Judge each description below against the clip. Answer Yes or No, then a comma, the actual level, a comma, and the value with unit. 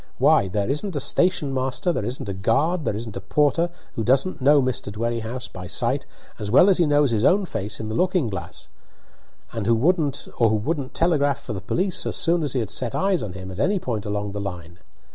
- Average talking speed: No, fast, 215 wpm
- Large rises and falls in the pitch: Yes, wide, 6.6 semitones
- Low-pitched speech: Yes, low, 125 Hz